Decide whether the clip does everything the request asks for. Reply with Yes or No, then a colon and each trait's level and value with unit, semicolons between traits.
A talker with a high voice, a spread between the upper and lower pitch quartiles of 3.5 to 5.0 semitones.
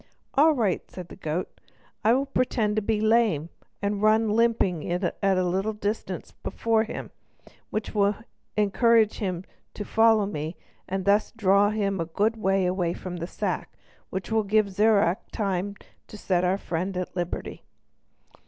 No: high, 200 Hz; average, 3.0 semitones